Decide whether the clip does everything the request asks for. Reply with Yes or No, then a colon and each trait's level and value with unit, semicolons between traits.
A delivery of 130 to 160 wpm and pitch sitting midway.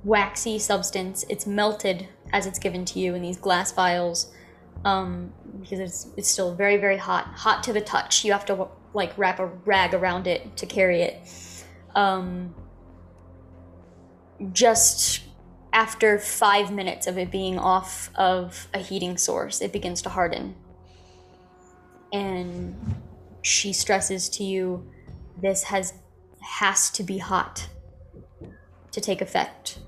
Yes: slow, 135 wpm; medium, 180 Hz